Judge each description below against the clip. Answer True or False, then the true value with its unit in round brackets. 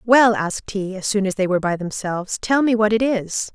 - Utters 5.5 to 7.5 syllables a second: True (5.6 syllables/s)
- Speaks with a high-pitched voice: True (205 Hz)